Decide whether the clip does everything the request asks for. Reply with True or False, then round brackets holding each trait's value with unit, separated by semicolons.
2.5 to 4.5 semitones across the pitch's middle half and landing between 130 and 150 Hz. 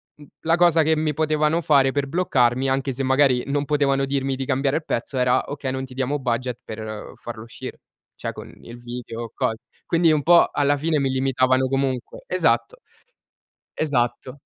True (2.8 semitones; 135 Hz)